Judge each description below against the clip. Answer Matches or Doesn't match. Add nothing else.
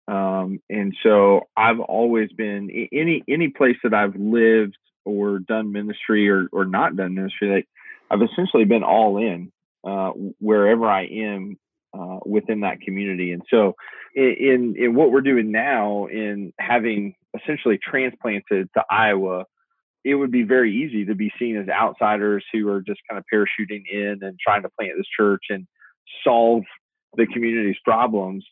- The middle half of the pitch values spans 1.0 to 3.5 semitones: Matches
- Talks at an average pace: Matches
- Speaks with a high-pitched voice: Doesn't match